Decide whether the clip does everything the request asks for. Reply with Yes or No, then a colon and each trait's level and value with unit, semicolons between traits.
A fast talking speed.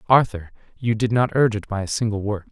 Yes: fast, 240 wpm